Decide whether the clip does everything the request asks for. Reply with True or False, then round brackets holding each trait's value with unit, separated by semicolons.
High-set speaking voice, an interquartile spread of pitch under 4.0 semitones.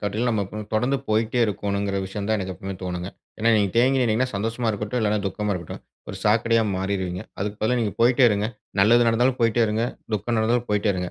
False (105 Hz; 2.7 semitones)